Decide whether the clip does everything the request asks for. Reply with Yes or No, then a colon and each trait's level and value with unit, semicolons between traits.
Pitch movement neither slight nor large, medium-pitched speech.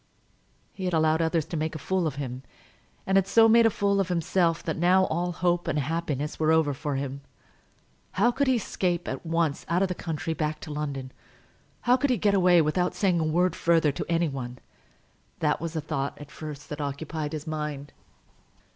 Yes: average, 3.3 semitones; medium, 165 Hz